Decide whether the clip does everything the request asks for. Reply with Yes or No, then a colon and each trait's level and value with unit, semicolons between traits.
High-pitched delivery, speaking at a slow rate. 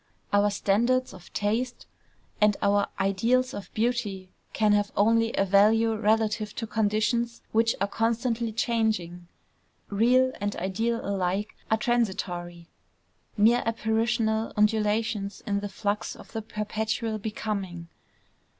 Yes: high, 215 Hz; slow, 120 wpm